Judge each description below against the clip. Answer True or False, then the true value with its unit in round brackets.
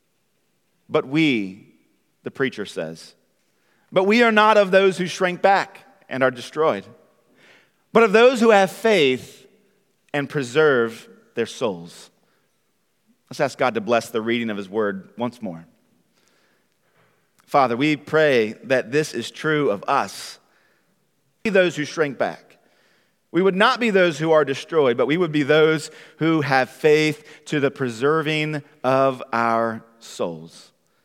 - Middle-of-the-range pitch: True (150 Hz)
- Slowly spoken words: False (150 wpm)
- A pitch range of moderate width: False (6.7 semitones)